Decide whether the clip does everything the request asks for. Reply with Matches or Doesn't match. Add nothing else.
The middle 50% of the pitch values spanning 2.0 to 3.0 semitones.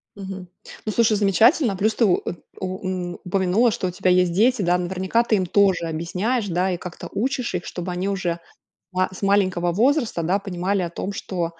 Matches